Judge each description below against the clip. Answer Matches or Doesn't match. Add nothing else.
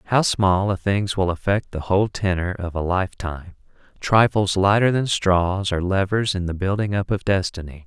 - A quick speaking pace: Doesn't match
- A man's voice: Matches